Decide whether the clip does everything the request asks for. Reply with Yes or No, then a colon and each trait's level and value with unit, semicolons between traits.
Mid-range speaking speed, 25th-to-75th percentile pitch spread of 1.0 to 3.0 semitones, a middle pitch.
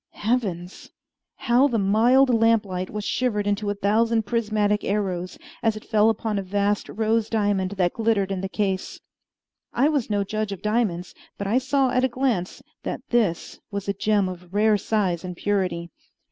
No: average, 175 wpm; average, 2.7 semitones; high, 210 Hz